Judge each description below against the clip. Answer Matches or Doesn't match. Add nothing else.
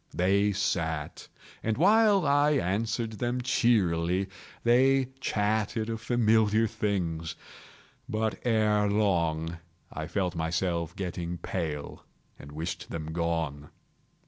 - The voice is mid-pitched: Doesn't match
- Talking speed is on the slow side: Matches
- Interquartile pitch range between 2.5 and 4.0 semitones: Doesn't match